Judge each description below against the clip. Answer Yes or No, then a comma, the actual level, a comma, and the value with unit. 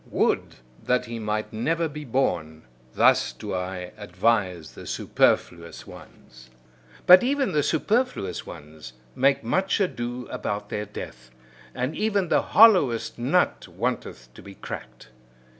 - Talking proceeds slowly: Yes, slow, 130 wpm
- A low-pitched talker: Yes, low, 115 Hz